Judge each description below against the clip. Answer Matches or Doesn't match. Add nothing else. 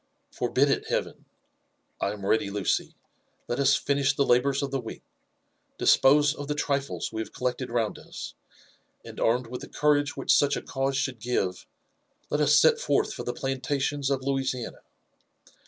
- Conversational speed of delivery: Matches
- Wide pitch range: Doesn't match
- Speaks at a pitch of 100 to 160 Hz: Matches